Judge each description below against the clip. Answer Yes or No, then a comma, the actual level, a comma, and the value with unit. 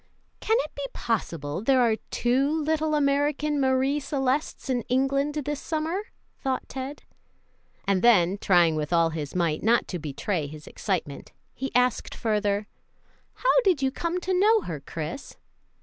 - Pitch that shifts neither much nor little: No, wide, 8.3 semitones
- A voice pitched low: No, very high, 260 Hz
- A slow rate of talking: No, average, 150 wpm